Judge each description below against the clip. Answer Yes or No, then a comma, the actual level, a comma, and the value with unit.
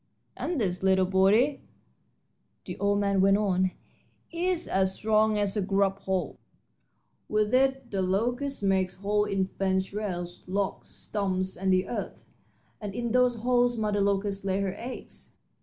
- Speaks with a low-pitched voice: No, high, 200 Hz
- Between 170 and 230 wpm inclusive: No, average, 150 wpm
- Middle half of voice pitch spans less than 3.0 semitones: Yes, narrow, 2.5 semitones